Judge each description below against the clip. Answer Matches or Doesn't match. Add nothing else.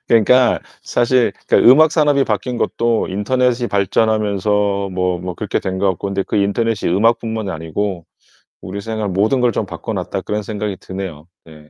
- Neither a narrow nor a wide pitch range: Matches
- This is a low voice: Matches